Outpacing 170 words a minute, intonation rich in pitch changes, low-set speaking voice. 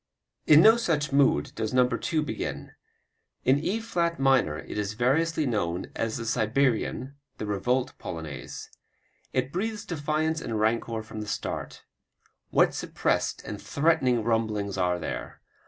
No: average, 140 wpm; wide, 6.1 semitones; low, 125 Hz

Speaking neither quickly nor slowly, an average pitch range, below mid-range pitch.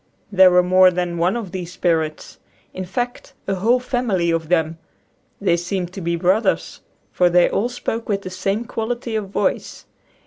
No: average, 175 wpm; average, 3.8 semitones; medium, 185 Hz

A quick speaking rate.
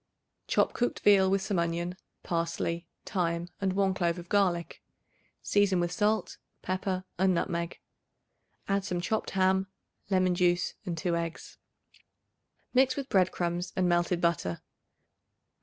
No: slow, 135 wpm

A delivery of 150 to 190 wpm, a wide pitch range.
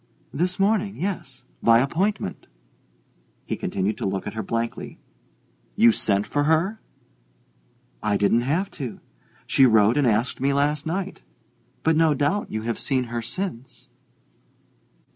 No: average, 140 wpm; wide, 6.6 semitones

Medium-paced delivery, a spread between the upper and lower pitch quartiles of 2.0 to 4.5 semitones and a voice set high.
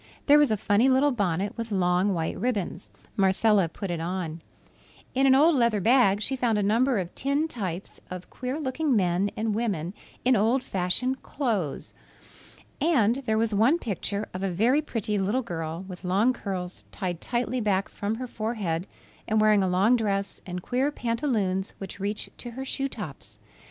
No: average, 175 wpm; average, 5.0 semitones; high, 210 Hz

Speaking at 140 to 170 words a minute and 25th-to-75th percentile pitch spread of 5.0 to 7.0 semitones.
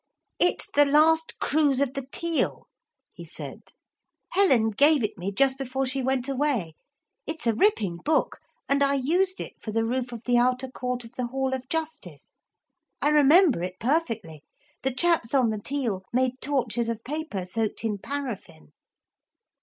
No: average, 165 wpm; average, 4.2 semitones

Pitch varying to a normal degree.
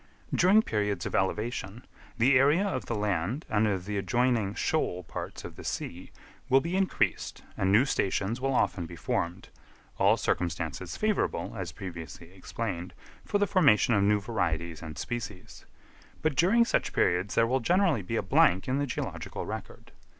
No: wide, 6.5 semitones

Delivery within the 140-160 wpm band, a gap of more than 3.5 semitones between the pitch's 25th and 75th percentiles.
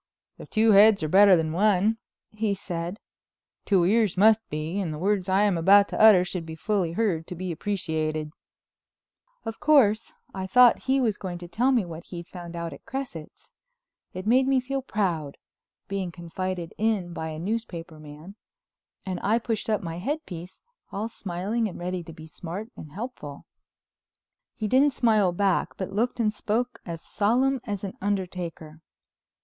No: average, 170 wpm; average, 4.3 semitones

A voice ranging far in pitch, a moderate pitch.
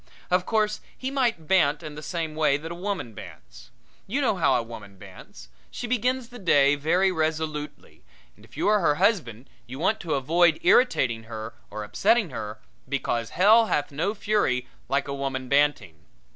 Yes: wide, 7.6 semitones; medium, 155 Hz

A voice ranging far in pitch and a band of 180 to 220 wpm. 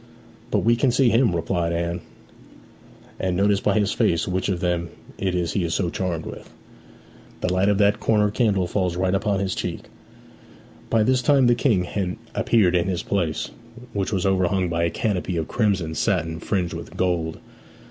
No: average, 3.0 semitones; average, 185 wpm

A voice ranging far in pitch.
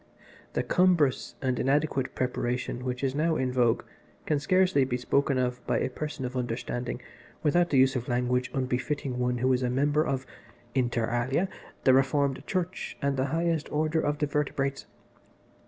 No: average, 2.8 semitones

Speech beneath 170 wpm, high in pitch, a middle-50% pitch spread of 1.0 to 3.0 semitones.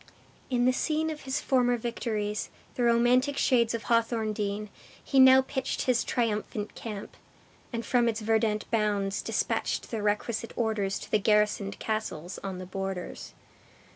Yes: average, 145 wpm; high, 225 Hz; average, 2.7 semitones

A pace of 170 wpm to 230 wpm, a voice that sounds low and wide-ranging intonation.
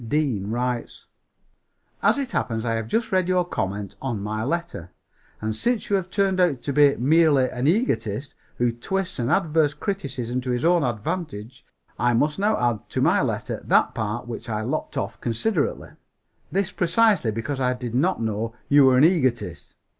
Yes: average, 175 wpm; low, 130 Hz; wide, 6.9 semitones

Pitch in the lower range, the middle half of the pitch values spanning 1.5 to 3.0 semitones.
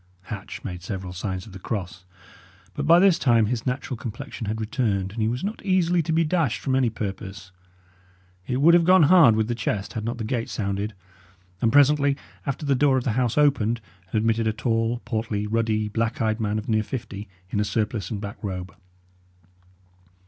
No: low, 115 Hz; average, 4.1 semitones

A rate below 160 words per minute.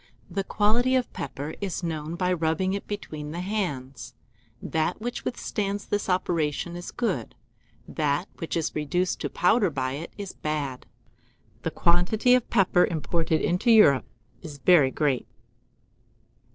Yes: average, 140 wpm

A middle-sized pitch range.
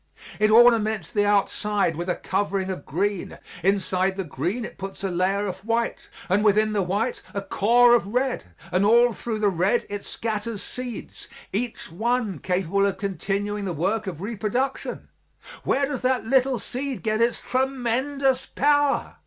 Yes: average, 3.7 semitones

